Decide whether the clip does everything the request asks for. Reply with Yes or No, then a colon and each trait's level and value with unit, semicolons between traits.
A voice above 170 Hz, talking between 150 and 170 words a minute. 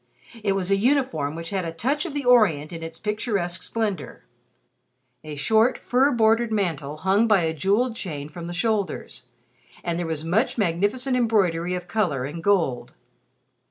Yes: high, 190 Hz; average, 165 wpm